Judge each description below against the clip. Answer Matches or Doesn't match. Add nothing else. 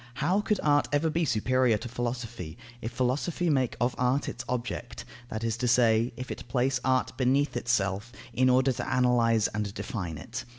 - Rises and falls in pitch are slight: Matches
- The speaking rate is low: Doesn't match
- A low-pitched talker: Matches